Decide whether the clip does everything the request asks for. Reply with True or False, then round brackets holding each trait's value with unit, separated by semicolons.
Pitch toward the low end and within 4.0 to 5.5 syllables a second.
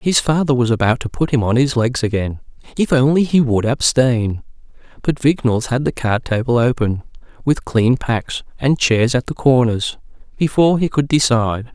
True (125 Hz; 5.0 syllables/s)